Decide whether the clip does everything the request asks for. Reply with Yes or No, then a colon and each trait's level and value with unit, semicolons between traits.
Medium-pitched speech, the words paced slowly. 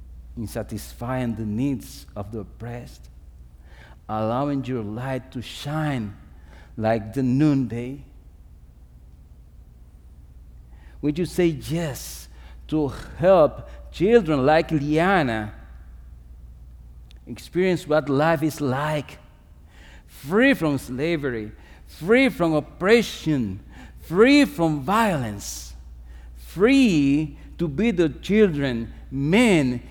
No: low, 115 Hz; slow, 90 wpm